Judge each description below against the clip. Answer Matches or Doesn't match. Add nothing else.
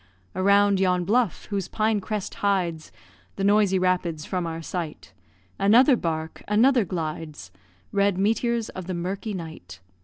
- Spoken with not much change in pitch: Doesn't match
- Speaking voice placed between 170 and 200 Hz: Matches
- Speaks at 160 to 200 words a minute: Doesn't match